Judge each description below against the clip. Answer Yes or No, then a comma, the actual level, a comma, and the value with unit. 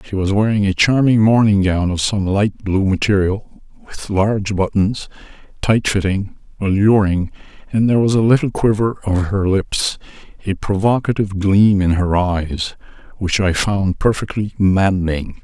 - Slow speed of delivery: No, average, 150 wpm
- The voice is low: Yes, low, 100 Hz